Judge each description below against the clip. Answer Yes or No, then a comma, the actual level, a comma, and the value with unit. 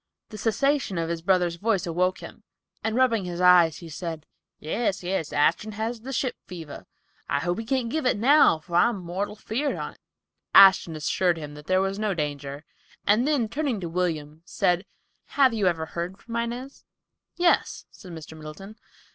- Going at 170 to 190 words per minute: Yes, average, 175 wpm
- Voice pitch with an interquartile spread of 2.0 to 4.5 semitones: No, wide, 5.4 semitones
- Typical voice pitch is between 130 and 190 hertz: Yes, medium, 185 Hz